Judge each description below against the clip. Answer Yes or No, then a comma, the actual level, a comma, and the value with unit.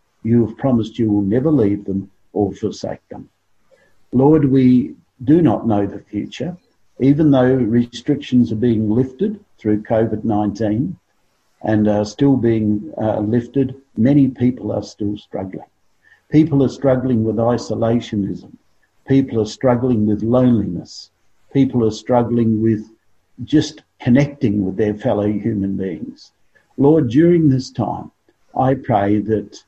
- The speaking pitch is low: Yes, low, 115 Hz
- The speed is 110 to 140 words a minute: Yes, slow, 135 wpm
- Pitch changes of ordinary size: Yes, average, 3.8 semitones